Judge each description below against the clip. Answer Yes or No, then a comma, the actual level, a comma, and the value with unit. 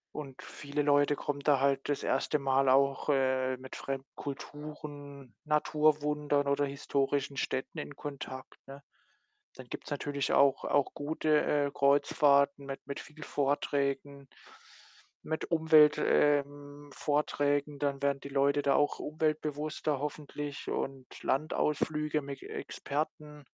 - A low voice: No, medium, 145 Hz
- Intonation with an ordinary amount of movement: No, narrow, 1.3 semitones